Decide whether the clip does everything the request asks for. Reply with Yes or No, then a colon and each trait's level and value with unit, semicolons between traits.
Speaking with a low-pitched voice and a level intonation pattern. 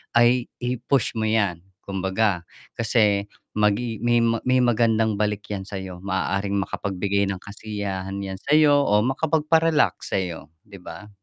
No: low, 105 Hz; average, 3.5 semitones